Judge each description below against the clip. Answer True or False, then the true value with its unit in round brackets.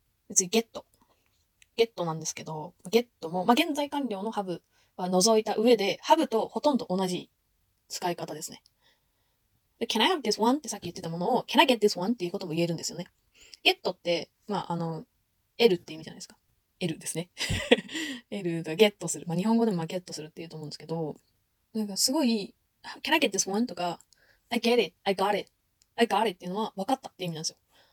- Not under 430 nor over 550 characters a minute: True (470 characters per minute)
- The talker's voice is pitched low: False (195 Hz)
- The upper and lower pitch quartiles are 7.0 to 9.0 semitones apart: False (5.2 semitones)